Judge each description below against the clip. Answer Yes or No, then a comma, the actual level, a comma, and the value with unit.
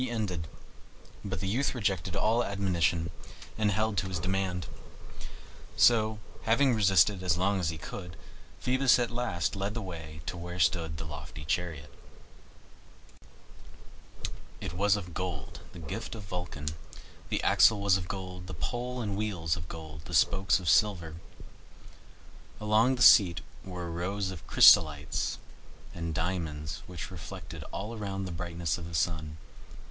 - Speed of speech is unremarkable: Yes, average, 150 wpm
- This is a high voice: No, very low, 90 Hz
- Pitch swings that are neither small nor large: Yes, average, 3.8 semitones